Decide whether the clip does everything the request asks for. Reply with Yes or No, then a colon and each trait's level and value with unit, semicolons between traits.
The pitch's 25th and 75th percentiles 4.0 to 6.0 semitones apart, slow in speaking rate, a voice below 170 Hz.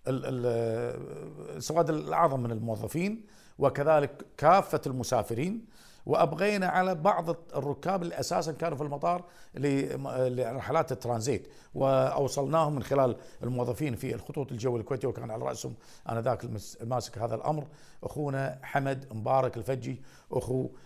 No: average, 4.4 semitones; average, 110 wpm; low, 135 Hz